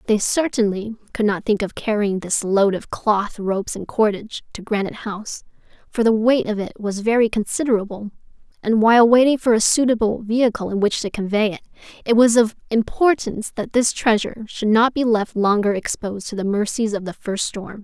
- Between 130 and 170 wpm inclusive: No, average, 190 wpm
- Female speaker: Yes, female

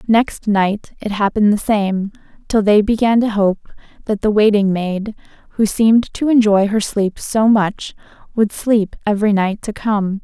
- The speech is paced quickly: No, average, 170 wpm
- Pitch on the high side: Yes, high, 210 Hz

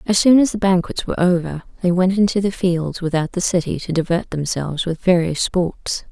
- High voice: No, medium, 180 Hz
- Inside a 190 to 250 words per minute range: Yes, fast, 205 wpm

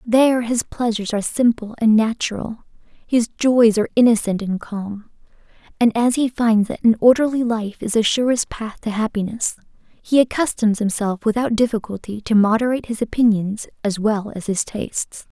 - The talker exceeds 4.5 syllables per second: Yes, 5.2 syllables/s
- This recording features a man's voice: No, female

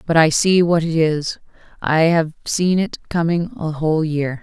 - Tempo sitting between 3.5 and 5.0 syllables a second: Yes, 4.3 syllables/s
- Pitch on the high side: No, medium, 160 Hz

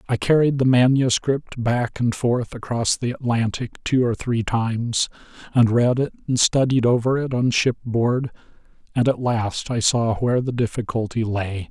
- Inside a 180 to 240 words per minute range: No, average, 165 wpm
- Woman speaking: No, male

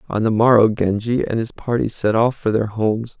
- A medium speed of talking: No, fast, 225 wpm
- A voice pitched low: Yes, low, 110 Hz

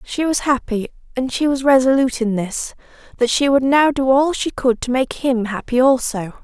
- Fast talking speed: No, average, 195 wpm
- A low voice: No, very high, 255 Hz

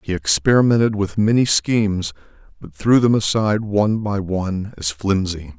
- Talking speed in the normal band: Yes, average, 150 wpm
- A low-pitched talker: Yes, low, 100 Hz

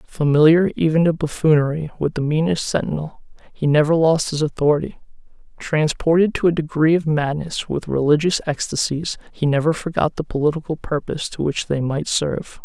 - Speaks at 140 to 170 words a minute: Yes, average, 155 wpm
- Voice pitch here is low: No, medium, 155 Hz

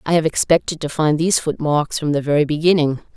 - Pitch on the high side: No, medium, 155 Hz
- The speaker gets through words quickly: Yes, fast, 210 wpm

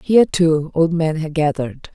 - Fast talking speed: No, average, 185 wpm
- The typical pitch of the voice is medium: Yes, medium, 160 Hz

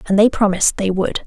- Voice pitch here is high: Yes, high, 200 Hz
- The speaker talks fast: Yes, fast, 235 wpm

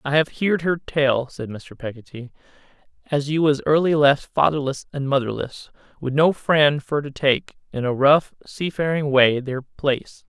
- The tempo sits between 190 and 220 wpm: No, average, 170 wpm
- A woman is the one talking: No, male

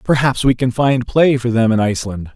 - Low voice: Yes, low, 125 Hz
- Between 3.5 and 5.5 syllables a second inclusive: Yes, 5.3 syllables/s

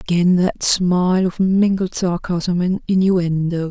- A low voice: No, medium, 180 Hz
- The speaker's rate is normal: No, slow, 130 wpm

